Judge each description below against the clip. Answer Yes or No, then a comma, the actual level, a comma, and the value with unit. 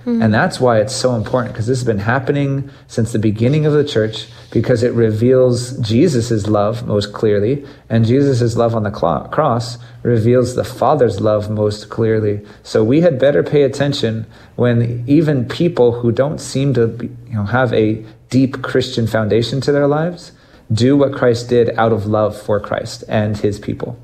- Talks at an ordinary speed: Yes, average, 180 wpm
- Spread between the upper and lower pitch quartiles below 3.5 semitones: Yes, average, 3.1 semitones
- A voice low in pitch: Yes, low, 120 Hz